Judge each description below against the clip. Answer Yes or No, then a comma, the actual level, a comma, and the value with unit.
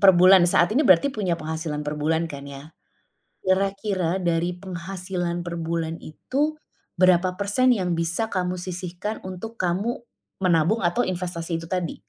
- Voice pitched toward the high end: No, medium, 180 Hz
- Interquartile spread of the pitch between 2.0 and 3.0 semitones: Yes, narrow, 2.6 semitones